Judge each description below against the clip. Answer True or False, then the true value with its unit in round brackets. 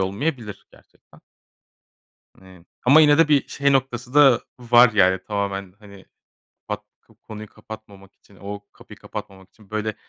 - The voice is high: False (105 Hz)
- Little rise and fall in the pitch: False (4.1 semitones)